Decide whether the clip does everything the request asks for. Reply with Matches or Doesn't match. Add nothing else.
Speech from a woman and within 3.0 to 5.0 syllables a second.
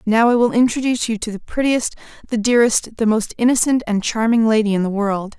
Doesn't match